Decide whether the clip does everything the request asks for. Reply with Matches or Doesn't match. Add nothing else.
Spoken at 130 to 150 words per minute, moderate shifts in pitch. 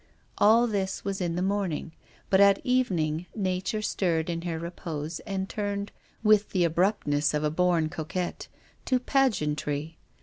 Matches